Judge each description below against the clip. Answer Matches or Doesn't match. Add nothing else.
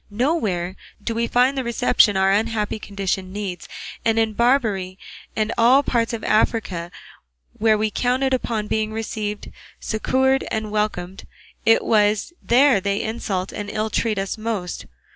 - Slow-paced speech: Doesn't match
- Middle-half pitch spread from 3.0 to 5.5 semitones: Doesn't match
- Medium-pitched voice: Doesn't match